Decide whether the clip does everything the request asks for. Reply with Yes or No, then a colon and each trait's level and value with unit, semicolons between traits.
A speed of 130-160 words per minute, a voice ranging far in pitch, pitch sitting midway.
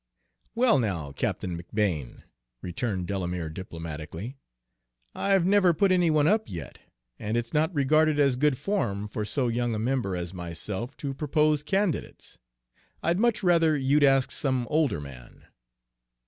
No: average, 145 wpm; wide, 8.7 semitones; low, 130 Hz